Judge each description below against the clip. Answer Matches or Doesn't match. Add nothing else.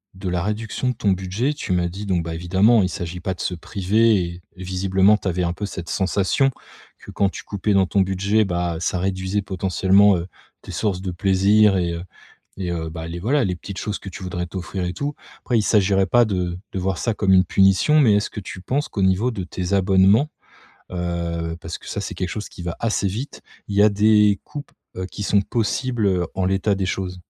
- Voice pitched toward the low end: Matches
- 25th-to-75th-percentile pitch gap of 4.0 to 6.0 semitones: Doesn't match